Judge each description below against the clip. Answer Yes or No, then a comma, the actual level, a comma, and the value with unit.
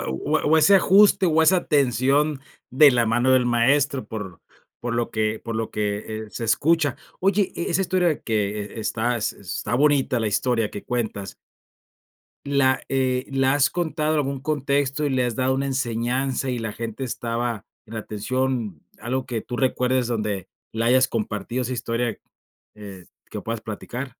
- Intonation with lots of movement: No, average, 3.7 semitones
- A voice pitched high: No, low, 125 Hz